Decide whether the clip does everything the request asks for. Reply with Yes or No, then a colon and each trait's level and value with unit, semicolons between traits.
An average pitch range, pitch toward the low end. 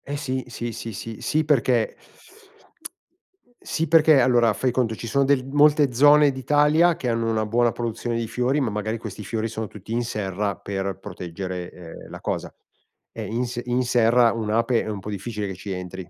Yes: average, 3.5 semitones; low, 115 Hz